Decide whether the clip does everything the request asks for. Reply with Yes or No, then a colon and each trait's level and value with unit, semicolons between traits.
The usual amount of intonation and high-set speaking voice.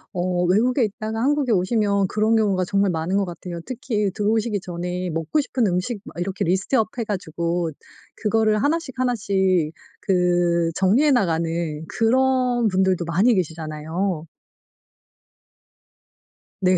Yes: average, 4.1 semitones; high, 195 Hz